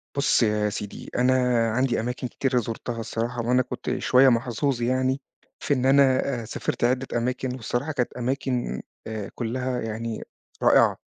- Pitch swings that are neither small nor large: No, narrow, 2.1 semitones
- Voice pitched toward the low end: Yes, low, 125 Hz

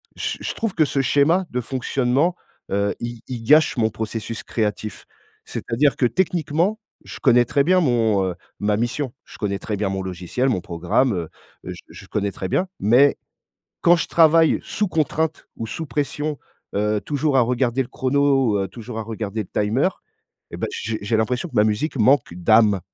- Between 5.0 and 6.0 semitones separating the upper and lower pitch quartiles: Yes, wide, 5.5 semitones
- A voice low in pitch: Yes, low, 120 Hz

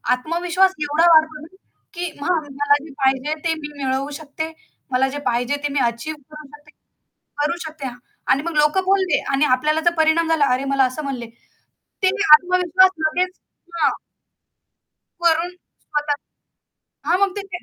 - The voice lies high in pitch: Yes, very high, 310 Hz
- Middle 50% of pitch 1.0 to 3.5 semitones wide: Yes, average, 3.2 semitones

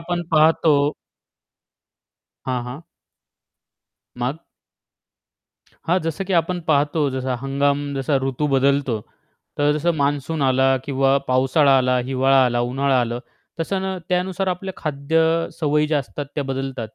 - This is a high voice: No, medium, 140 Hz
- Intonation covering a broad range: No, average, 3.1 semitones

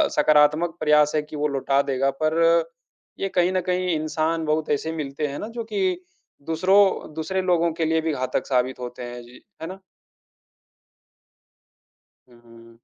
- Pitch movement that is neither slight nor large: Yes, average, 3.3 semitones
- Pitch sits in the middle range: Yes, medium, 155 Hz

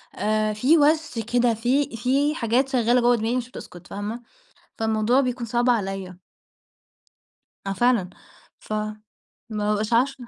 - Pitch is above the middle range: Yes, high, 235 Hz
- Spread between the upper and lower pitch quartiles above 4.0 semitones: No, average, 2.9 semitones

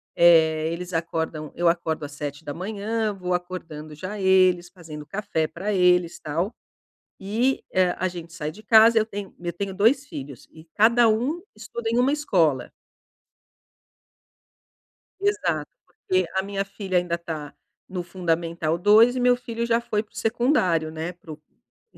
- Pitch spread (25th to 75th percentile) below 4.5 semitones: No, average, 4.8 semitones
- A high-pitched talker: No, medium, 180 Hz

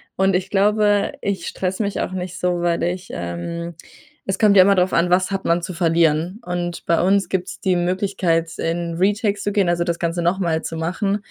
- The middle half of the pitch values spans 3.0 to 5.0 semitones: No, narrow, 2.4 semitones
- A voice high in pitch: No, medium, 180 Hz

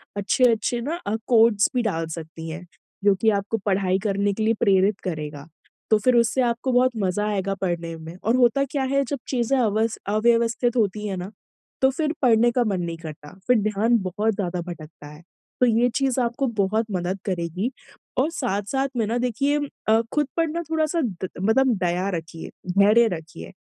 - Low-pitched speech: No, high, 215 Hz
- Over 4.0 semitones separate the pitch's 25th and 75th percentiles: Yes, average, 4.7 semitones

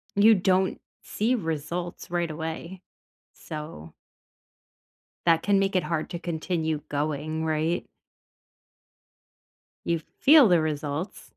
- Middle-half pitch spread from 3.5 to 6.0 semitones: No, average, 2.9 semitones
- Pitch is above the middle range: No, medium, 165 Hz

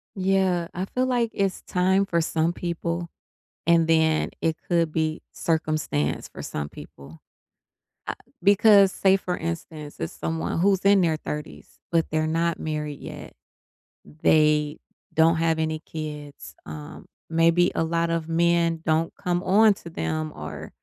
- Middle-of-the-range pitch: Yes, medium, 165 Hz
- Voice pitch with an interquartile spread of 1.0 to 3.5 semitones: Yes, narrow, 2.4 semitones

